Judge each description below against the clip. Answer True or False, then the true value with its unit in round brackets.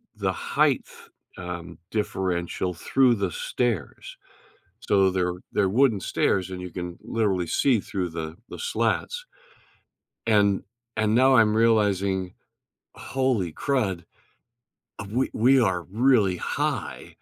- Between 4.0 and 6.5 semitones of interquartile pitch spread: True (5.0 semitones)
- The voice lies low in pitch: True (100 Hz)